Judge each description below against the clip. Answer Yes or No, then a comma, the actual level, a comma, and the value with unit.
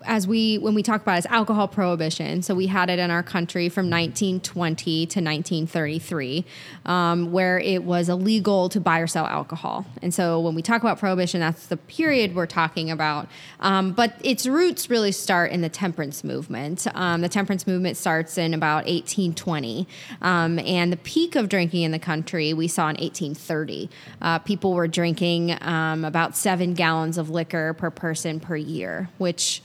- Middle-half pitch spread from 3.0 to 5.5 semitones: No, narrow, 2.5 semitones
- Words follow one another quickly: No, average, 180 wpm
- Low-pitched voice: No, medium, 175 Hz